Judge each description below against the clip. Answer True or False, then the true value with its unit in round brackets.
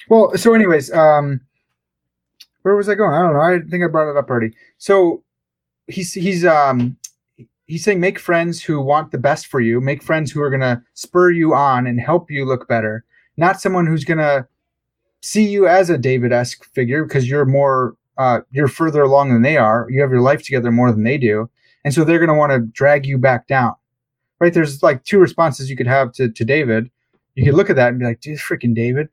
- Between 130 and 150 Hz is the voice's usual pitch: True (140 Hz)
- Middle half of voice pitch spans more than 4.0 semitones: True (5.0 semitones)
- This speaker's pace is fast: True (220 wpm)